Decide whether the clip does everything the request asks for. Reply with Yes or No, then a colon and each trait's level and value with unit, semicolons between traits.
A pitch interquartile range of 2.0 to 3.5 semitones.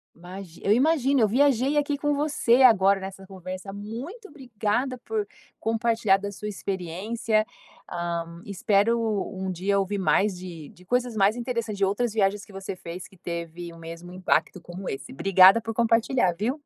No: average, 4.2 semitones